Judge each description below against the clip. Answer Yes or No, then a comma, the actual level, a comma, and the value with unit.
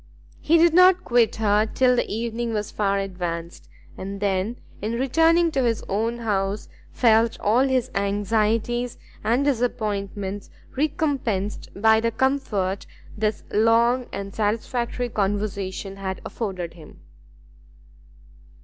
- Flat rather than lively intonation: No, average, 3.5 semitones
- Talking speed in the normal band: No, slow, 120 wpm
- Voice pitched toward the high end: Yes, high, 220 Hz